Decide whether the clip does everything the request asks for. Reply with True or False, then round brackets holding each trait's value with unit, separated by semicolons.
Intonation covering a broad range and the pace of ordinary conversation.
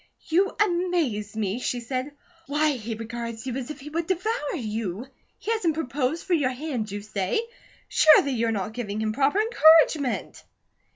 True (6.2 semitones; 165 wpm)